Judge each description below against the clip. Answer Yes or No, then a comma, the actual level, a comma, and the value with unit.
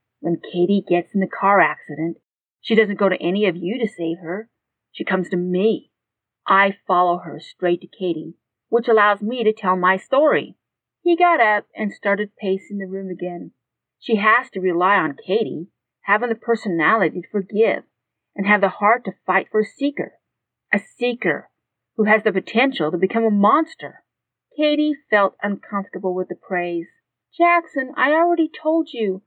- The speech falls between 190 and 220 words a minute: No, average, 170 wpm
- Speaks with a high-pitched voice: Yes, high, 200 Hz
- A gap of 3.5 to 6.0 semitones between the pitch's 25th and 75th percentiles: Yes, average, 3.9 semitones